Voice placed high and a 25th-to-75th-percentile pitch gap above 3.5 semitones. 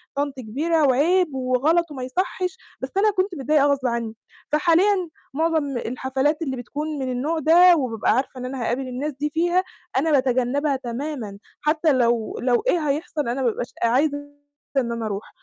Yes: very high, 280 Hz; average, 4.0 semitones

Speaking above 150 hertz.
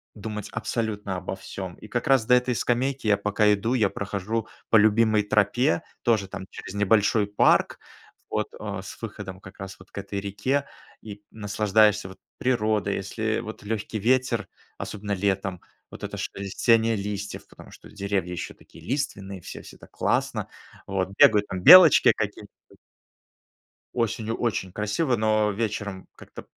No: low, 105 Hz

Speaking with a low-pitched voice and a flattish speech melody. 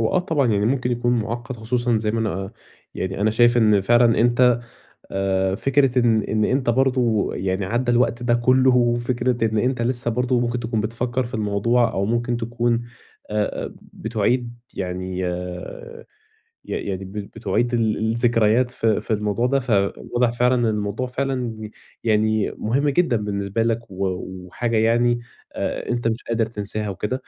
Yes: low, 115 Hz; narrow, 2.3 semitones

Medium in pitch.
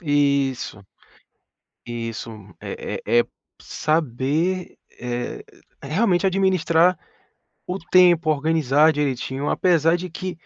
Yes: medium, 155 Hz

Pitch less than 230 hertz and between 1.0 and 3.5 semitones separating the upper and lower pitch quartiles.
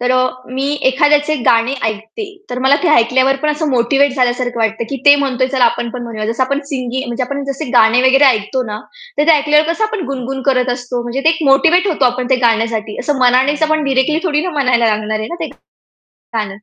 No: very high, 260 Hz; average, 3.2 semitones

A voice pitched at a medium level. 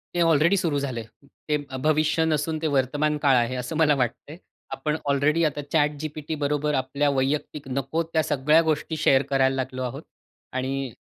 Yes: medium, 145 Hz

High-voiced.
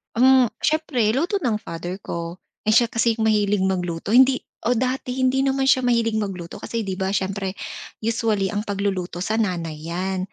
Yes: high, 215 Hz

